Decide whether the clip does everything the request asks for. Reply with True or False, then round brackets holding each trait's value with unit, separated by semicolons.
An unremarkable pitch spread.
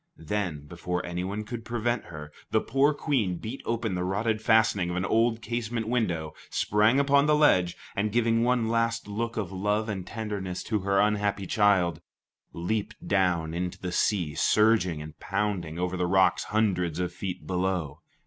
True (4.1 semitones)